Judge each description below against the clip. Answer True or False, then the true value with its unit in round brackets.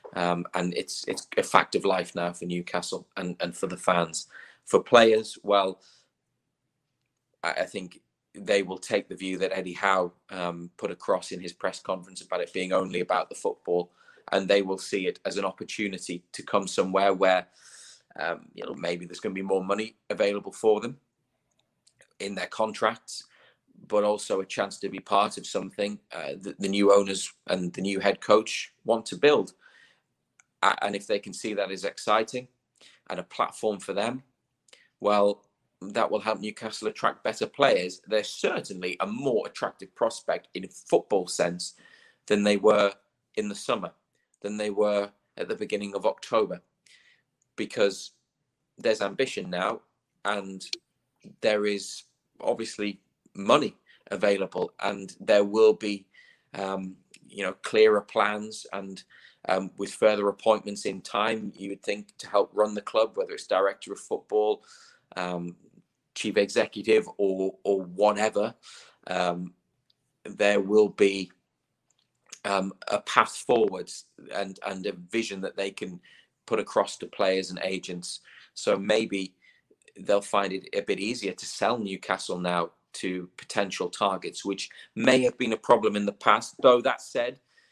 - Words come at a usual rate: True (160 wpm)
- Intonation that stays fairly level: True (2.2 semitones)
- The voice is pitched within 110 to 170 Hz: False (100 Hz)